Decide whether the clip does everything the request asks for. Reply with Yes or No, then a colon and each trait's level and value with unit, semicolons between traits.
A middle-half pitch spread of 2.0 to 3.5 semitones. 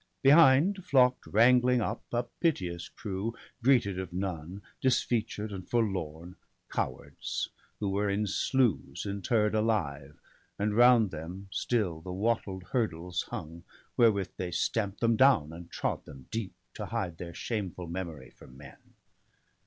No: average, 5.1 semitones